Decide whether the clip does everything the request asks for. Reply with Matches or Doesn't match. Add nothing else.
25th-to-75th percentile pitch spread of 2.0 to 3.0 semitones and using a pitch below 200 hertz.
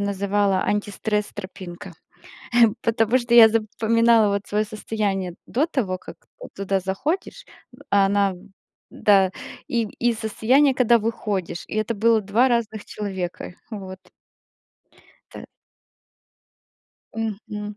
Doesn't match